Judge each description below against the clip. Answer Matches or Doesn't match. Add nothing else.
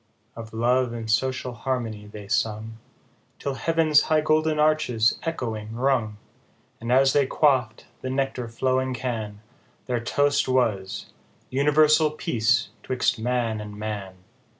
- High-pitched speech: Doesn't match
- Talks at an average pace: Doesn't match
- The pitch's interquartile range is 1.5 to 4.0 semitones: Matches